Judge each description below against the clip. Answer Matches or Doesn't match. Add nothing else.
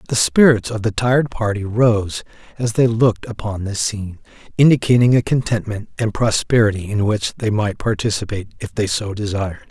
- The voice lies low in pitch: Matches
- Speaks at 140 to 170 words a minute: Matches